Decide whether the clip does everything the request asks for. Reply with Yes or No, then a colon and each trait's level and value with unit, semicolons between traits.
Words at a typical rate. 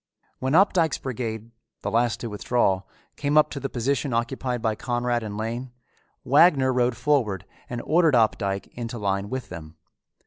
Yes: average, 160 wpm